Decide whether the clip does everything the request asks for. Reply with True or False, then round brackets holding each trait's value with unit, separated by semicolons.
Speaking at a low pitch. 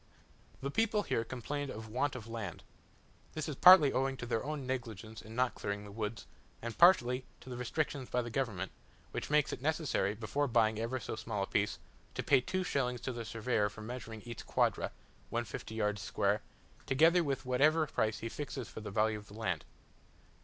True (120 Hz)